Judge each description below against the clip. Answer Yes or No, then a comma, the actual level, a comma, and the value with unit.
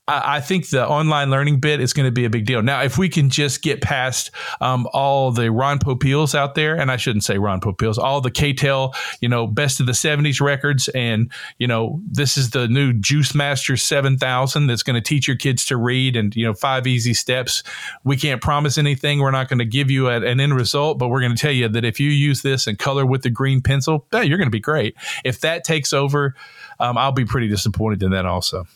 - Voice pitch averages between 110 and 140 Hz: Yes, low, 135 Hz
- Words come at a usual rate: No, fast, 240 wpm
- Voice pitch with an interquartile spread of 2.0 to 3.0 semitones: Yes, average, 2.7 semitones